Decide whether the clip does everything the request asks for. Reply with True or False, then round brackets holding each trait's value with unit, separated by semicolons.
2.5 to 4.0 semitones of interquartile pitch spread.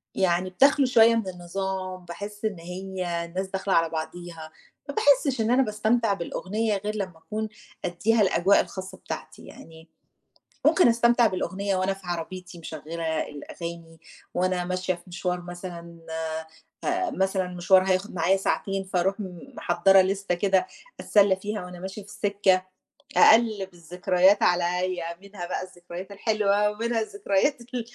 True (2.8 semitones)